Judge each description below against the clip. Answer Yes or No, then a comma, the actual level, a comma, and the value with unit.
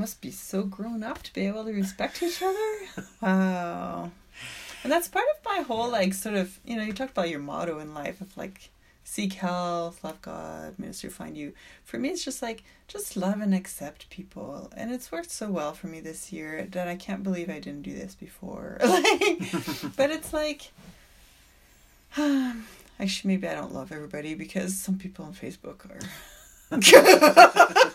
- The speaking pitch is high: Yes, high, 195 Hz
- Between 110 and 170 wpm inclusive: No, average, 185 wpm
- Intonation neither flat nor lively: No, wide, 7.3 semitones